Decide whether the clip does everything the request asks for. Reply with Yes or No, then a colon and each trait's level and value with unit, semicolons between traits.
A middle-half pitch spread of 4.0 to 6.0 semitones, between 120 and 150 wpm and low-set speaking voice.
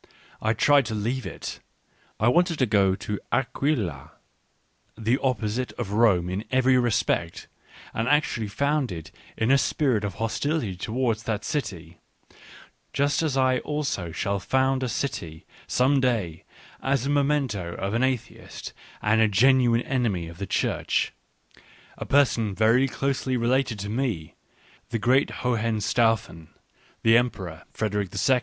Yes: average, 4.4 semitones; average, 140 wpm; low, 115 Hz